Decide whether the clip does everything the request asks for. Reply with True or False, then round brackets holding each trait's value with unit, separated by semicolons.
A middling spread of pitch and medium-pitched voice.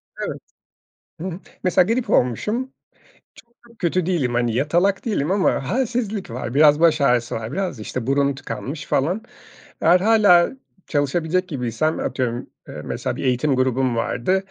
False (6.6 semitones; 155 Hz)